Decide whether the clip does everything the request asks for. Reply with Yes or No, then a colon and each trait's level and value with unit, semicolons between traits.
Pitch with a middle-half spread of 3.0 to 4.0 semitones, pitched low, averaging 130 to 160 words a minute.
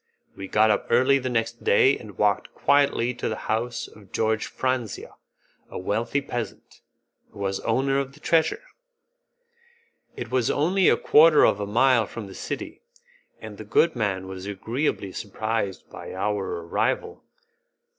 No: average, 4.4 semitones; low, 115 Hz; average, 155 wpm